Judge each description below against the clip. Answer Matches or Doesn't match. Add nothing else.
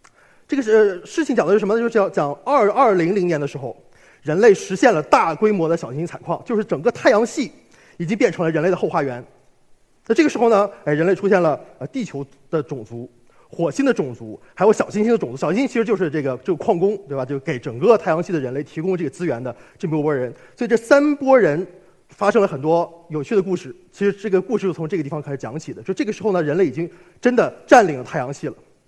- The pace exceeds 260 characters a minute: Matches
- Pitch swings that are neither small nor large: Doesn't match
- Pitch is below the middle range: Doesn't match